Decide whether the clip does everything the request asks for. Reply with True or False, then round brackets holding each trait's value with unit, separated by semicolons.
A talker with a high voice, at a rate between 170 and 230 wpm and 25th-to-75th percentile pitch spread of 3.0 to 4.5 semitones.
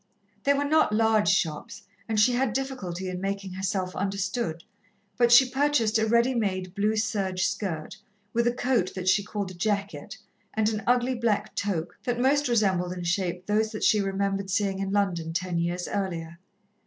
True (200 Hz; 180 wpm; 3.9 semitones)